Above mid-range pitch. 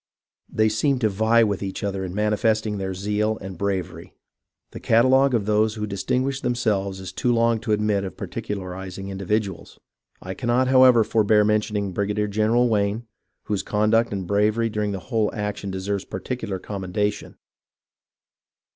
No: low, 105 Hz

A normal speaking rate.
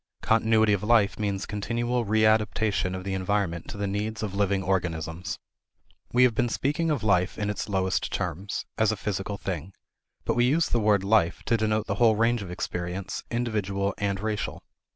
Yes: average, 180 wpm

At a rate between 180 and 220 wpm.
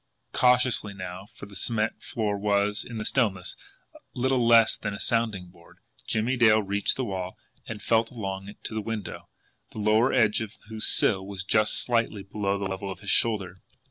Yes: average, 185 wpm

